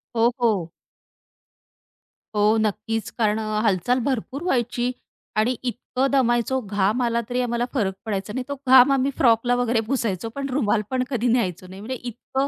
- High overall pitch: Yes, high, 240 Hz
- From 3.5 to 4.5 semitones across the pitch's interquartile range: No, average, 3.1 semitones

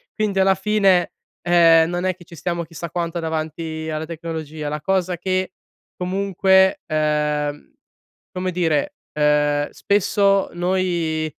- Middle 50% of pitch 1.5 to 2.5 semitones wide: No, average, 2.9 semitones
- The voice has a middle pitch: Yes, medium, 170 Hz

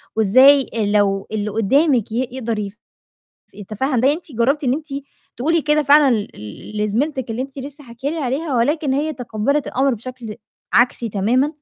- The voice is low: No, very high, 255 Hz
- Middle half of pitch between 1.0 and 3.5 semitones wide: No, average, 4.3 semitones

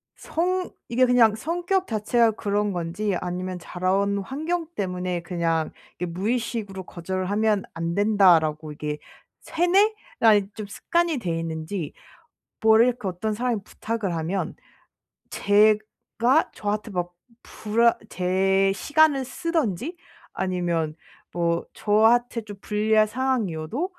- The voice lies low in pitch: No, high, 210 Hz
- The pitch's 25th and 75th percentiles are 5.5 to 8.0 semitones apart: No, average, 5.1 semitones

